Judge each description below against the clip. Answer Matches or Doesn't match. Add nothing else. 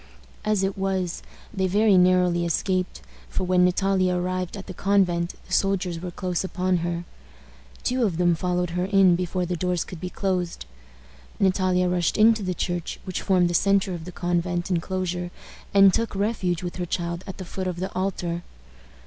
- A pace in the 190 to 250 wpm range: Doesn't match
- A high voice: Doesn't match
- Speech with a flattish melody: Matches